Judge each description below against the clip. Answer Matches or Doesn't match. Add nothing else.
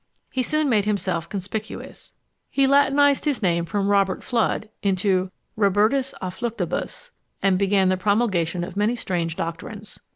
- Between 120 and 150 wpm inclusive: Matches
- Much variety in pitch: Doesn't match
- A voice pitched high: Matches